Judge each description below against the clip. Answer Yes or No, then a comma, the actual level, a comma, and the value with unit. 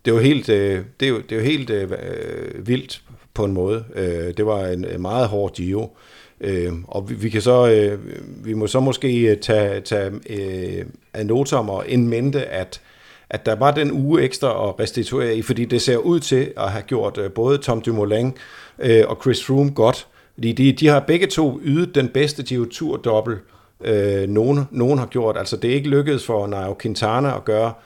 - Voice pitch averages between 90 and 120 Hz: Yes, low, 115 Hz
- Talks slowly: No, average, 175 wpm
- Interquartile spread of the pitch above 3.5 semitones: Yes, average, 4.3 semitones